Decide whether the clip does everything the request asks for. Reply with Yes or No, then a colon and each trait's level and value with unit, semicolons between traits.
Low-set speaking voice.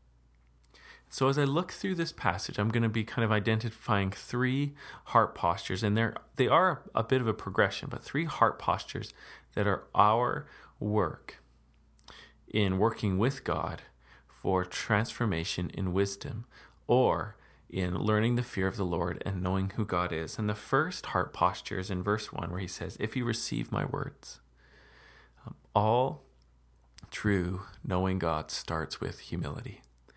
Yes: low, 100 Hz